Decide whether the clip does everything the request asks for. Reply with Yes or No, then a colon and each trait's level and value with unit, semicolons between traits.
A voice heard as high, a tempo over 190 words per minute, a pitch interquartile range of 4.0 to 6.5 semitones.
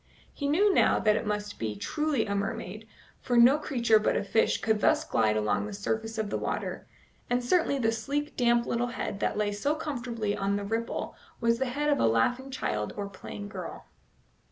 Yes: high, 225 Hz; fast, 205 wpm; average, 4.5 semitones